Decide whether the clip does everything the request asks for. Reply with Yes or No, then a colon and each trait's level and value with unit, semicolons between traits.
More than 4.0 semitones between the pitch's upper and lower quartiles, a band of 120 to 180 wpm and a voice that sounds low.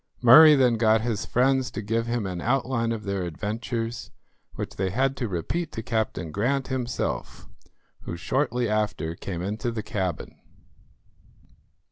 No: average, 3.7 semitones; average, 145 wpm; low, 115 Hz